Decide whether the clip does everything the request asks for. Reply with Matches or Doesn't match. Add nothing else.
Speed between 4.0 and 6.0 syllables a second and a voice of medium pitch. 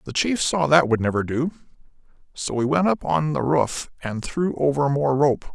Matches